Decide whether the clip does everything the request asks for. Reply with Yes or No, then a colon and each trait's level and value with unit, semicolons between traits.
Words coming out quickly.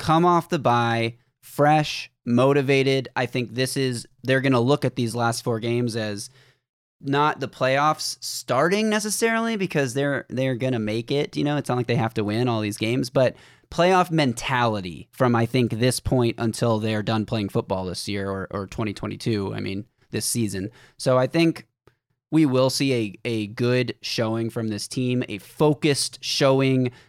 No: average, 175 wpm